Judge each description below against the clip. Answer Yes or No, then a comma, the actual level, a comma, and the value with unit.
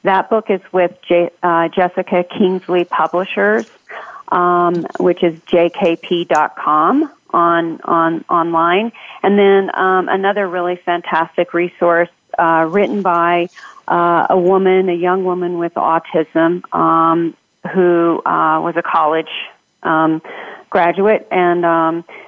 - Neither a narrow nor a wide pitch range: No, narrow, 1.9 semitones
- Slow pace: Yes, slow, 120 wpm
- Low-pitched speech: No, medium, 175 Hz